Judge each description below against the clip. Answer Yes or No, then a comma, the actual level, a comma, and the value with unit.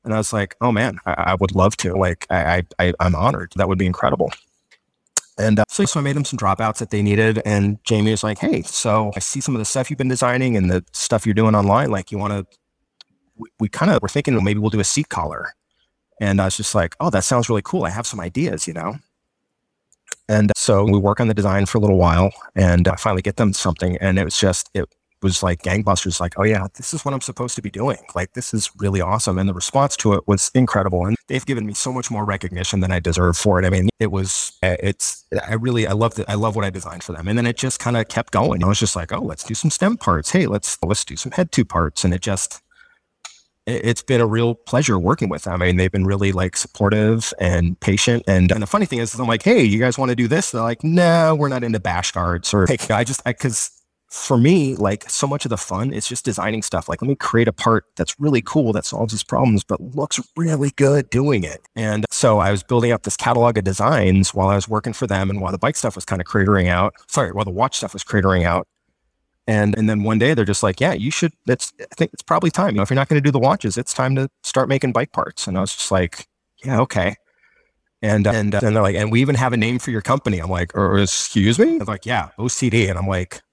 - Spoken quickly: Yes, fast, 270 wpm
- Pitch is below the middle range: Yes, low, 105 Hz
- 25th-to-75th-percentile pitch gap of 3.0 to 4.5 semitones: Yes, average, 4.1 semitones